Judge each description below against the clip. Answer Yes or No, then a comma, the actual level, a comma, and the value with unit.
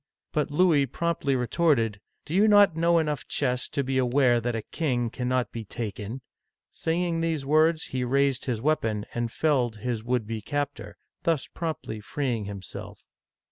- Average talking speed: Yes, average, 170 wpm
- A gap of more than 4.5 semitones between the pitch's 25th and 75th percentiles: Yes, average, 4.9 semitones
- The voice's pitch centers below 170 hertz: Yes, low, 135 Hz